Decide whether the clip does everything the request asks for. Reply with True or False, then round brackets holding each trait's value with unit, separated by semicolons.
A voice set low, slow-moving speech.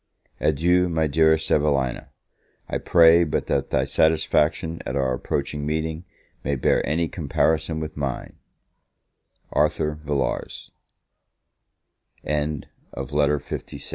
True (75 Hz; 120 wpm)